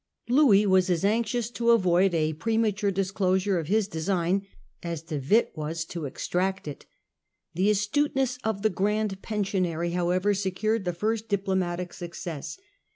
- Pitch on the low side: No, high, 190 Hz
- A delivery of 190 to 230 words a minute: No, average, 150 wpm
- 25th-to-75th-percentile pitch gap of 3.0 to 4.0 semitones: Yes, average, 3.5 semitones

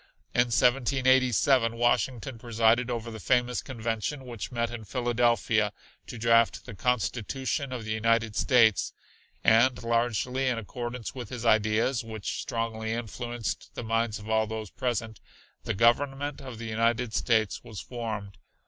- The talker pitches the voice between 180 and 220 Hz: No, low, 115 Hz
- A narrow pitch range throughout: Yes, narrow, 2.0 semitones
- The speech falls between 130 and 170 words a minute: Yes, average, 140 wpm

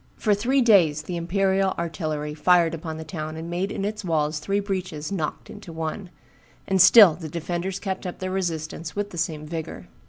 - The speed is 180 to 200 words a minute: Yes, average, 190 wpm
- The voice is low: No, medium, 175 Hz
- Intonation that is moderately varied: Yes, average, 3.4 semitones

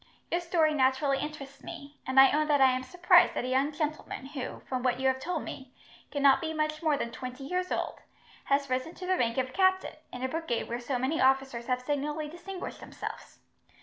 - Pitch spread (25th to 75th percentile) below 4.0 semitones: Yes, average, 3.0 semitones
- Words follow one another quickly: Yes, fast, 215 wpm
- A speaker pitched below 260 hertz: No, very high, 275 Hz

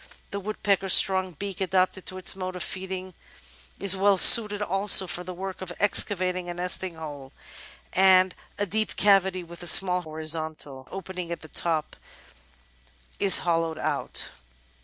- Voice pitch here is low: No, medium, 185 Hz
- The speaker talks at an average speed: Yes, average, 150 wpm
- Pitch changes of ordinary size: No, narrow, 2.0 semitones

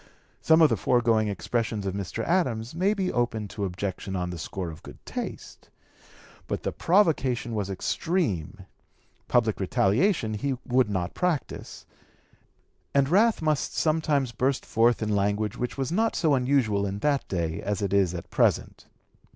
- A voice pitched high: No, low, 115 Hz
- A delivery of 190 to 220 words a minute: No, average, 160 wpm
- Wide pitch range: Yes, wide, 6.6 semitones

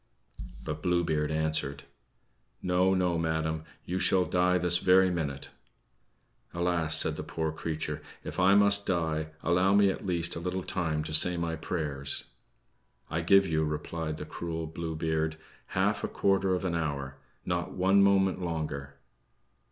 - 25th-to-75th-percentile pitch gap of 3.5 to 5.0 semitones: No, average, 2.7 semitones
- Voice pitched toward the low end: Yes, very low, 85 Hz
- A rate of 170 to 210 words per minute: No, average, 155 wpm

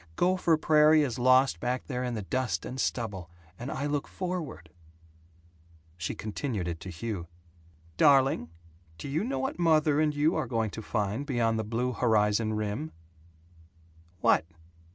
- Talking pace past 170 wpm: No, average, 155 wpm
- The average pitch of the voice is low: Yes, low, 125 Hz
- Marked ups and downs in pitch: Yes, wide, 5.9 semitones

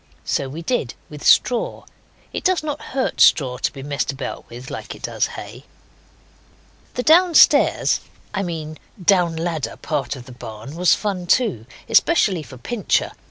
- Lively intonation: Yes, wide, 7.8 semitones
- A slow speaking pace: No, average, 160 wpm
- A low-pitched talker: No, medium, 165 Hz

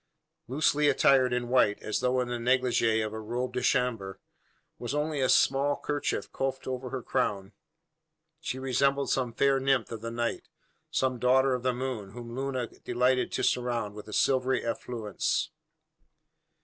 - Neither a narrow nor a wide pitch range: No, narrow, 2.1 semitones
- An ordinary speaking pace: Yes, average, 160 wpm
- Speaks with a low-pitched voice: Yes, low, 125 Hz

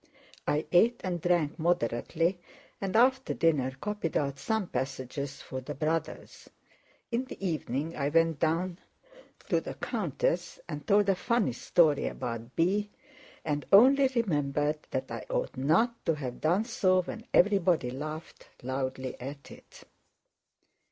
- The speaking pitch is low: No, medium, 165 Hz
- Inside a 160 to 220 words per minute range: No, average, 140 wpm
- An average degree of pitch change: No, wide, 6.1 semitones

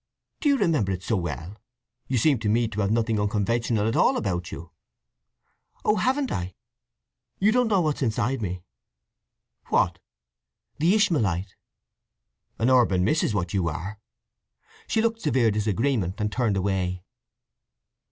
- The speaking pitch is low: Yes, low, 110 Hz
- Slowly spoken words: No, average, 145 wpm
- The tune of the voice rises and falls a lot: Yes, wide, 6.7 semitones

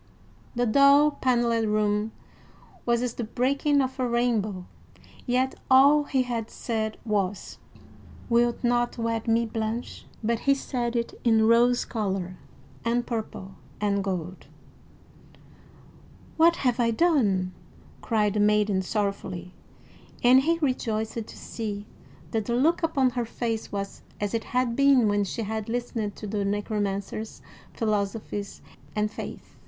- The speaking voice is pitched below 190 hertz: No, high, 230 Hz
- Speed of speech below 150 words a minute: Yes, slow, 135 wpm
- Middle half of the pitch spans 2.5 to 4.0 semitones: Yes, average, 3.0 semitones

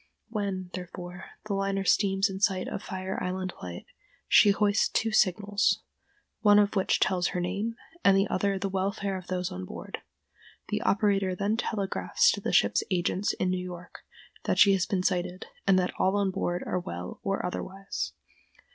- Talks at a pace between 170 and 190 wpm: Yes, average, 175 wpm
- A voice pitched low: No, high, 190 Hz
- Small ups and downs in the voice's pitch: Yes, narrow, 1.7 semitones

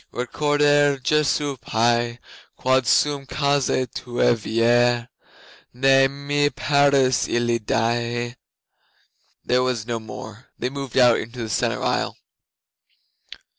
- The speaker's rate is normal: No, slow, 105 wpm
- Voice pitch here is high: No, low, 125 Hz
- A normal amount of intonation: Yes, average, 3.0 semitones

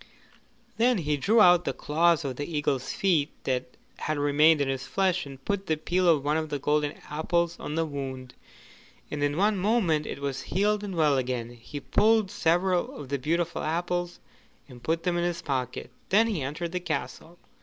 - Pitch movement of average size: Yes, average, 3.8 semitones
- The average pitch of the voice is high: No, medium, 160 Hz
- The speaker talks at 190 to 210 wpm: Yes, average, 195 wpm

